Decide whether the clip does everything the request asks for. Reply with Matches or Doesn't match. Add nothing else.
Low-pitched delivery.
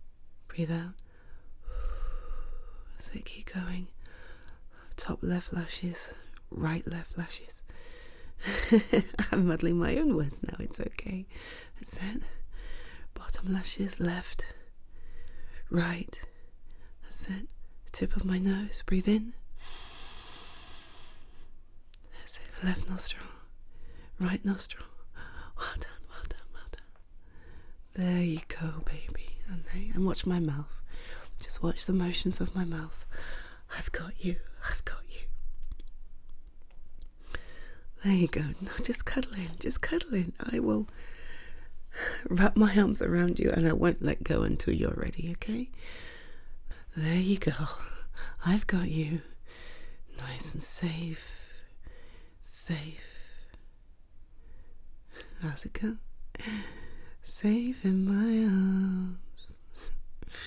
Doesn't match